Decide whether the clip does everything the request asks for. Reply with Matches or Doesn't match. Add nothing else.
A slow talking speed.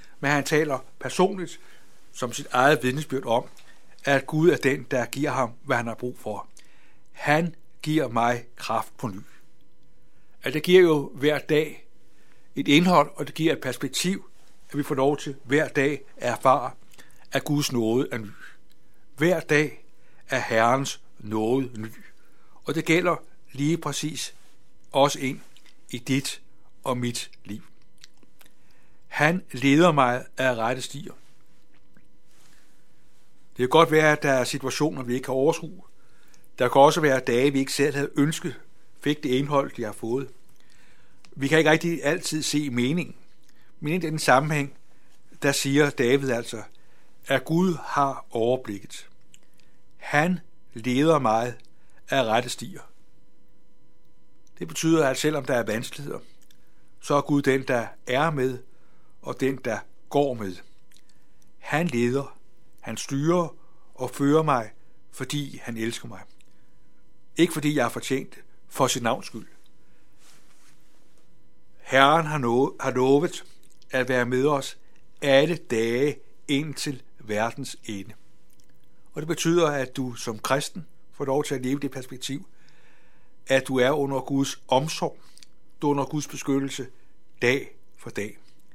Matches